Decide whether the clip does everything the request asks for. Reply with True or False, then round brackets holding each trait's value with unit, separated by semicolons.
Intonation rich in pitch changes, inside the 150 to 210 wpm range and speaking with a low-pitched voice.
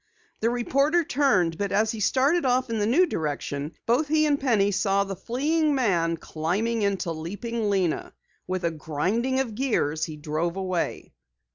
False (7.3 semitones; 165 wpm; 210 Hz)